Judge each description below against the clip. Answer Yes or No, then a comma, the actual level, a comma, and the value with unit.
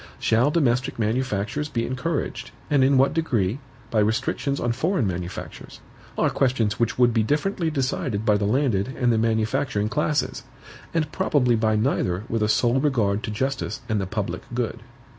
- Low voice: Yes, low, 120 Hz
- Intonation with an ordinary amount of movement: Yes, average, 4.3 semitones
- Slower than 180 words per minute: Yes, average, 165 wpm